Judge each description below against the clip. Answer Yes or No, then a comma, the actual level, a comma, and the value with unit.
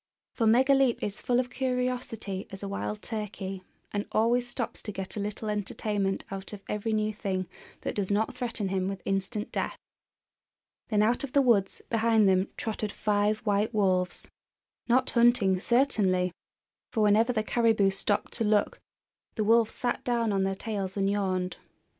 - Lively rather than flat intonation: No, average, 3.0 semitones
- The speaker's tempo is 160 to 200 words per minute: Yes, average, 165 wpm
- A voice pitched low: No, high, 210 Hz